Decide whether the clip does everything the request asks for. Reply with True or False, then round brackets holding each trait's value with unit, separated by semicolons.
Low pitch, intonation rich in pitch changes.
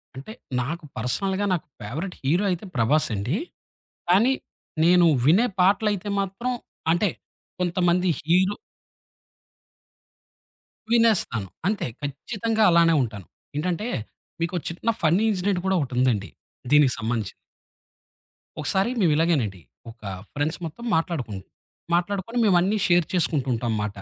False (170 Hz; 6.4 semitones)